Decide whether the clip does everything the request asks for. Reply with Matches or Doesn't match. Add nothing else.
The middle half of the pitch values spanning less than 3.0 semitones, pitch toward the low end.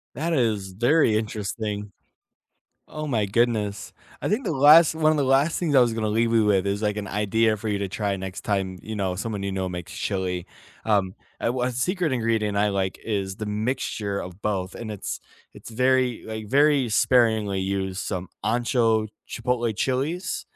Doesn't match